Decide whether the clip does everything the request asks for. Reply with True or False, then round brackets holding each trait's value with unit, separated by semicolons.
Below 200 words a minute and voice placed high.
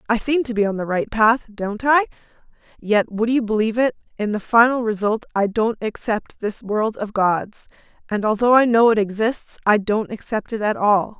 False (205 wpm; 220 Hz)